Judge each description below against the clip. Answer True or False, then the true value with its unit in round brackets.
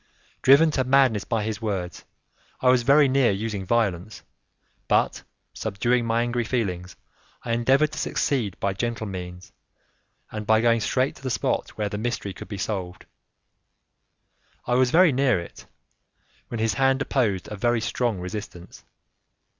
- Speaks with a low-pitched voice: True (115 Hz)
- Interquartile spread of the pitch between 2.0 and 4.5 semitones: True (4.2 semitones)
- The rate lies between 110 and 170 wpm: True (155 wpm)